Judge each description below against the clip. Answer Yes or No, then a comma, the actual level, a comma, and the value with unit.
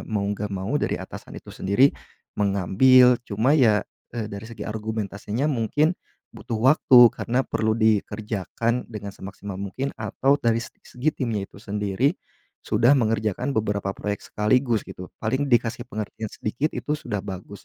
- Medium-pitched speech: No, low, 110 Hz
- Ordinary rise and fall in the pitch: Yes, average, 3.5 semitones